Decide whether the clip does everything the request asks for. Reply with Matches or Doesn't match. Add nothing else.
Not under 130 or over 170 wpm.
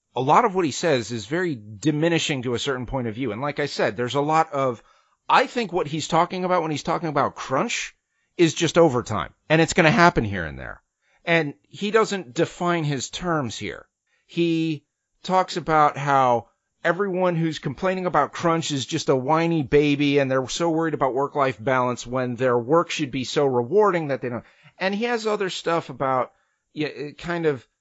Doesn't match